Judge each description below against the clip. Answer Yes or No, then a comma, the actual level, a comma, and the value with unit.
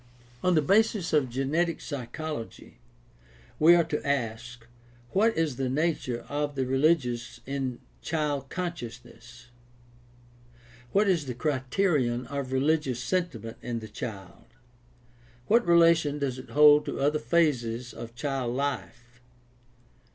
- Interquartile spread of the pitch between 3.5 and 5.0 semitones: Yes, average, 4.7 semitones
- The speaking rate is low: Yes, slow, 125 wpm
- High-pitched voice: No, medium, 140 Hz